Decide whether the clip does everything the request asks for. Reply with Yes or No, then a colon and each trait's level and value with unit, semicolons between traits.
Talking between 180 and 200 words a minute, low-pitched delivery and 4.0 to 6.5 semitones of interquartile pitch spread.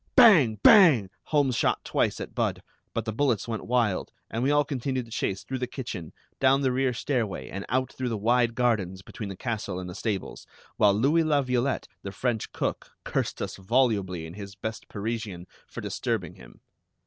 Yes: average, 190 wpm; low, 115 Hz; average, 4.5 semitones